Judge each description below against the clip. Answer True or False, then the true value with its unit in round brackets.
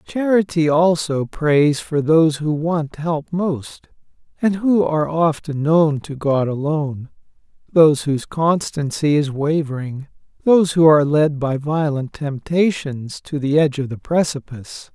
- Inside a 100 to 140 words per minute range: True (135 wpm)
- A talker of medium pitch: True (150 Hz)